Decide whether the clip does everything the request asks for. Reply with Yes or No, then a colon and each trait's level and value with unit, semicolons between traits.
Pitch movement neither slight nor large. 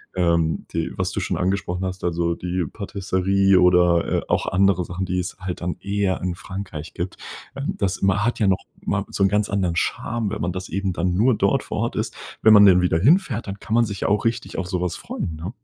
No: narrow, 2.1 semitones